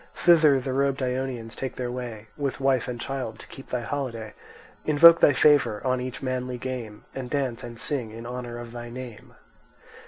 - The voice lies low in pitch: Yes, low, 125 Hz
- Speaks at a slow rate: No, average, 185 wpm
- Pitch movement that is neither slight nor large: No, narrow, 2.3 semitones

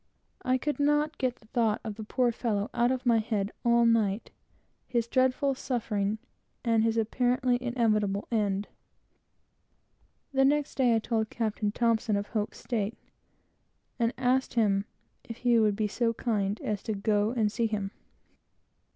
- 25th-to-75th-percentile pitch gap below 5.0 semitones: Yes, average, 2.8 semitones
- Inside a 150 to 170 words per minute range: Yes, average, 160 wpm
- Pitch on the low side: No, high, 230 Hz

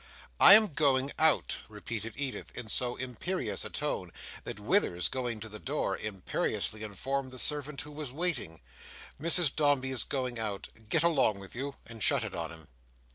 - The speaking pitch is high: No, low, 130 Hz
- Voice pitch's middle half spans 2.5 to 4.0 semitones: No, average, 5.2 semitones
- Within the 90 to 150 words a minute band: No, average, 175 wpm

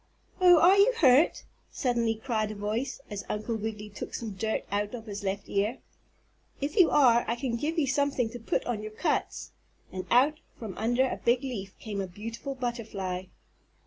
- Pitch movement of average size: Yes, average, 4.1 semitones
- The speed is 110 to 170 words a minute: No, average, 185 wpm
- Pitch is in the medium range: No, high, 230 Hz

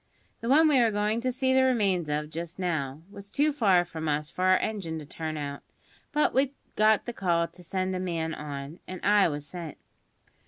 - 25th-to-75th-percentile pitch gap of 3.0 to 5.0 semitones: No, wide, 5.4 semitones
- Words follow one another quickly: Yes, fast, 210 wpm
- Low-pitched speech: No, medium, 185 Hz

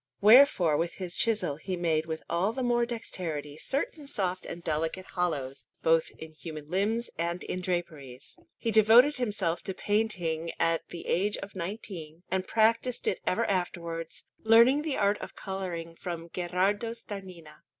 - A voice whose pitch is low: No, medium, 185 Hz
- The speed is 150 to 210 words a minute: Yes, average, 155 wpm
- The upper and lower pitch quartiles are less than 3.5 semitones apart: No, average, 4.7 semitones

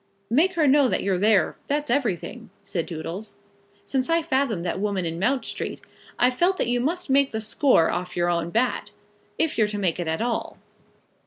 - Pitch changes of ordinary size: No, wide, 7.2 semitones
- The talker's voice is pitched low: No, high, 230 Hz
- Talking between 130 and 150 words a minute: No, average, 195 wpm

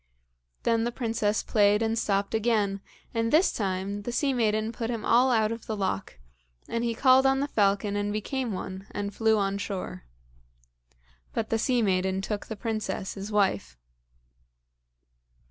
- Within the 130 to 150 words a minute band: No, average, 165 wpm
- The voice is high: Yes, high, 215 Hz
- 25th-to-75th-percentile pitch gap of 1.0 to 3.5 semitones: Yes, narrow, 2.5 semitones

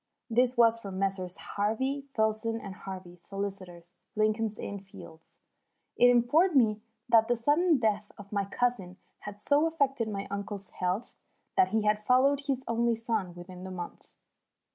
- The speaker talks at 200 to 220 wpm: No, average, 155 wpm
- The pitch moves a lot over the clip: No, average, 3.8 semitones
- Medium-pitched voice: No, high, 215 Hz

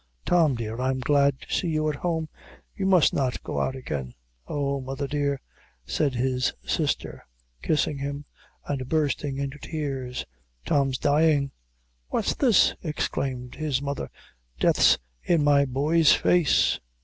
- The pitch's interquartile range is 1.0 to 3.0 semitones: Yes, narrow, 2.6 semitones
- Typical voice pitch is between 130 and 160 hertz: Yes, medium, 140 Hz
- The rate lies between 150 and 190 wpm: No, average, 140 wpm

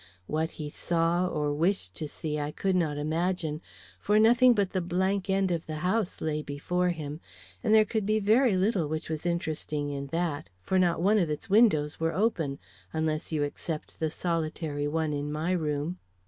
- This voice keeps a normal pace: Yes, average, 190 wpm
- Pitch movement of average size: Yes, average, 3.8 semitones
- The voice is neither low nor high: Yes, medium, 165 Hz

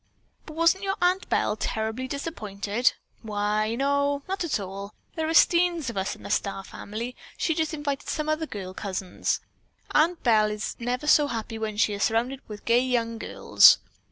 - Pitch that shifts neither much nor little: No, wide, 6.4 semitones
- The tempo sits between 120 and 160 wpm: No, average, 185 wpm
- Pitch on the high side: Yes, high, 240 Hz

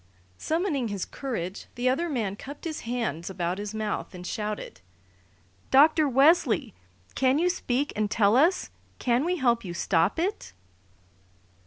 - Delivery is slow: No, average, 145 wpm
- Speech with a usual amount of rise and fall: No, wide, 6.4 semitones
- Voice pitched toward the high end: Yes, high, 245 Hz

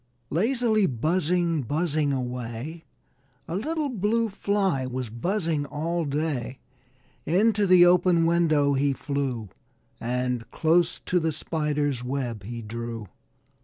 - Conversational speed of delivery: No, slow, 115 wpm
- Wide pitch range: Yes, wide, 5.8 semitones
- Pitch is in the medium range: Yes, medium, 155 Hz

